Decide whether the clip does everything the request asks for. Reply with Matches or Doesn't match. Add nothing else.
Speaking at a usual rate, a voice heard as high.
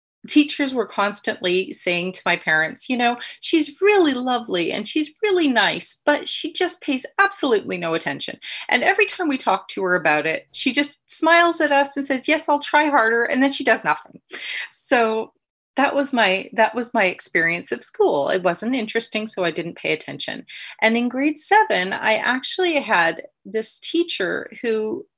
Matches